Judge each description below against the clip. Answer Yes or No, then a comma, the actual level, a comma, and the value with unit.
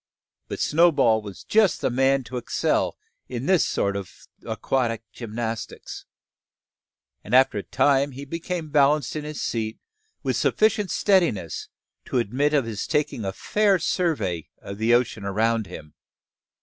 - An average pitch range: No, wide, 5.7 semitones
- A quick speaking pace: No, average, 145 wpm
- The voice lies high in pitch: No, low, 130 Hz